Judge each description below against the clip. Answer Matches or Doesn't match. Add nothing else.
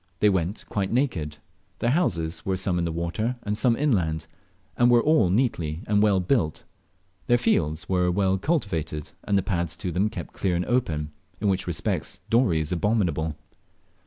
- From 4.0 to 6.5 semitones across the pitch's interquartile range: Matches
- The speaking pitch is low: Matches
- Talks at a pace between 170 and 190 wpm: Matches